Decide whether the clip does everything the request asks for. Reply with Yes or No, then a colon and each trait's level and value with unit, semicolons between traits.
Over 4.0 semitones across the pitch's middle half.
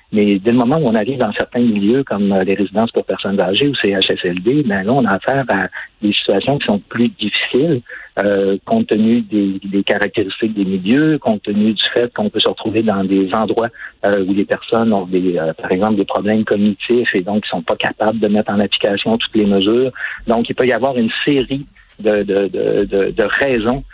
No: average, 3.2 semitones